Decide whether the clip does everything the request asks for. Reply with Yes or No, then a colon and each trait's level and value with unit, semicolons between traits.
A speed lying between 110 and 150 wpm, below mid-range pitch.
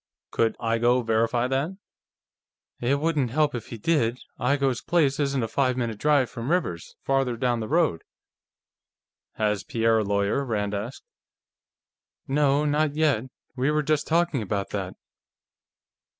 Yes: average, 140 wpm; low, 125 Hz